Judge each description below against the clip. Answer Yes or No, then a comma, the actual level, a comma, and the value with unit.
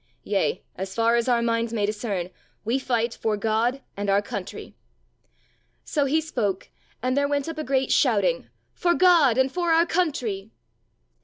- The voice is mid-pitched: No, high, 240 Hz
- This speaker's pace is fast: No, average, 165 wpm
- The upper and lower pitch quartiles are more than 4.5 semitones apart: Yes, average, 5.1 semitones